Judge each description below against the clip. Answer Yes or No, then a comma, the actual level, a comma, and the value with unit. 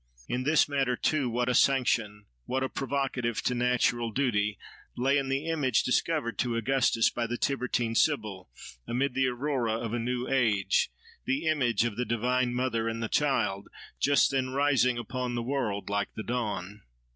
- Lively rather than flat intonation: No, average, 2.8 semitones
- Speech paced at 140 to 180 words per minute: Yes, average, 170 wpm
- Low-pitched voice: Yes, low, 125 Hz